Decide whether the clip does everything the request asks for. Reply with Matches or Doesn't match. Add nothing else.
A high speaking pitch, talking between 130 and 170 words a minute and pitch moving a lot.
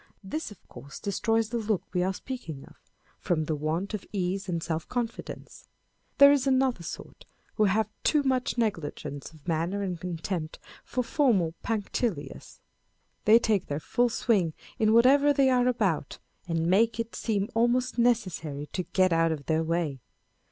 Matches